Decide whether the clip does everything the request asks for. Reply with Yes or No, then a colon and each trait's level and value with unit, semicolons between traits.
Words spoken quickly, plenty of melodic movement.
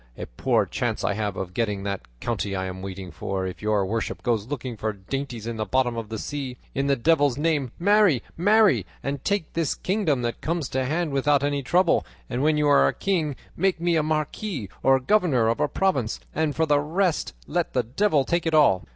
Yes: fast, 210 wpm; wide, 6.4 semitones